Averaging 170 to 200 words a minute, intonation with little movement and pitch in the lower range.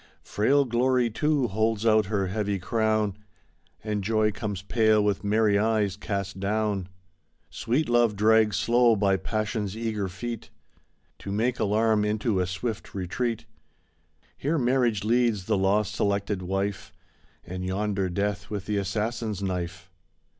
No: slow, 135 wpm; narrow, 2.3 semitones; low, 105 Hz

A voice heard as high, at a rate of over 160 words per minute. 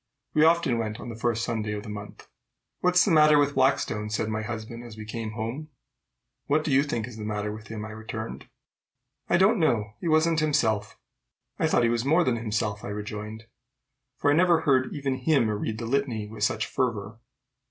No: low, 115 Hz; fast, 205 wpm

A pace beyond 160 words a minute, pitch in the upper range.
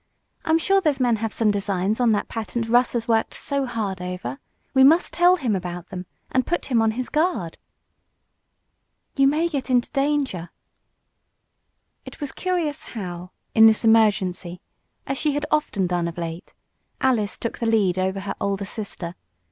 Yes: average, 170 wpm; high, 225 Hz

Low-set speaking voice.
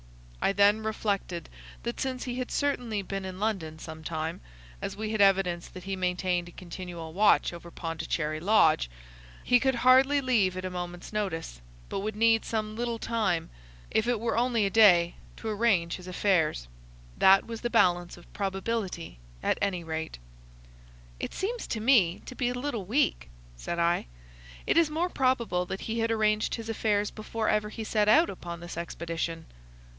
No: high, 195 Hz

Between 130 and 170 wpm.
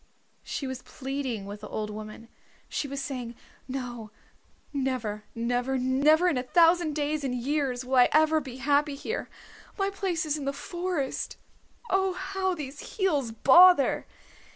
Yes: average, 155 wpm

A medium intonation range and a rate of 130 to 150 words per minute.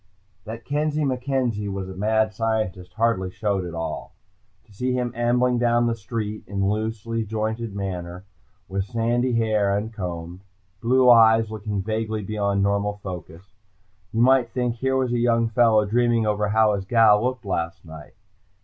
No: average, 3.1 semitones; average, 160 wpm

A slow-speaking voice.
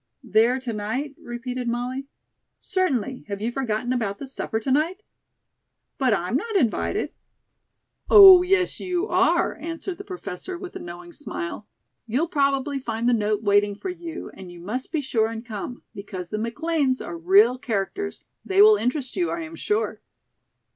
No: average, 165 wpm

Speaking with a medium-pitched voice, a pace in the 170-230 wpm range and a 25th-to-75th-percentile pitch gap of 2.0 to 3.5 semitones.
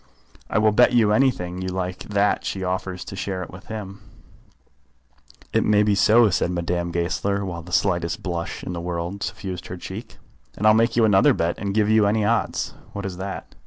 No: very low, 95 Hz; average, 200 wpm; average, 2.9 semitones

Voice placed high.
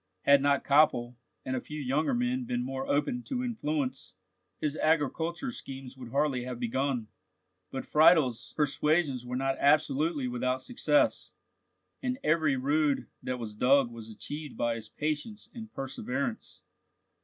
No: medium, 140 Hz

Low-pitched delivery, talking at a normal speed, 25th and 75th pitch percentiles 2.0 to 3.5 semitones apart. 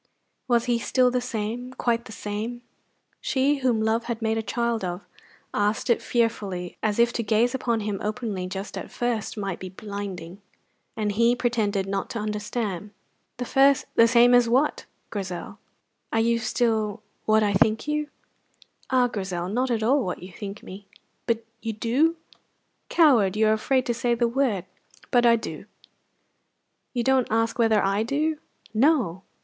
No: high, 225 Hz; average, 165 wpm; average, 2.9 semitones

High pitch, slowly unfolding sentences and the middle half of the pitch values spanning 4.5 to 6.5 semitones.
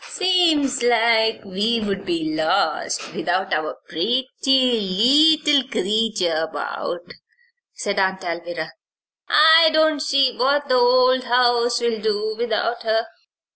Yes: high, 240 Hz; slow, 110 wpm; average, 5.1 semitones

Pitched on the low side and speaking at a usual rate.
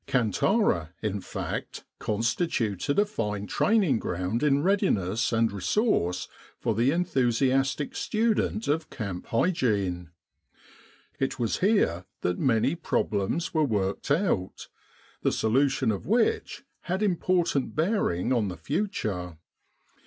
No: low, 125 Hz; slow, 115 wpm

